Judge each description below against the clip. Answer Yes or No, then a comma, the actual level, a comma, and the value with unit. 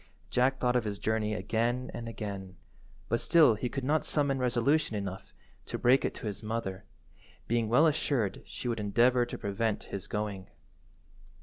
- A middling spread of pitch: Yes, average, 3.3 semitones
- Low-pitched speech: Yes, low, 115 Hz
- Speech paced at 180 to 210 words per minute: No, average, 170 wpm